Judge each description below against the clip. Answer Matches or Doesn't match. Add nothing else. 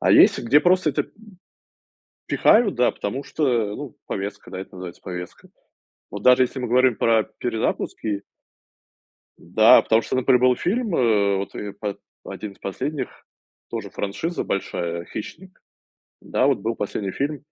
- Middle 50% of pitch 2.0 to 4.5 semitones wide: Doesn't match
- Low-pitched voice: Matches